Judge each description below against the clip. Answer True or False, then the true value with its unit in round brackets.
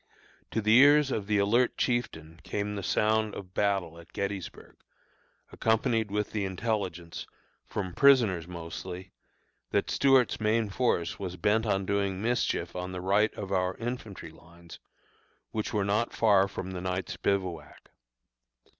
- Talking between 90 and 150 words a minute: True (145 wpm)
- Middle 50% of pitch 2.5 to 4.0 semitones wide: True (3.2 semitones)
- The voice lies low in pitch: True (100 Hz)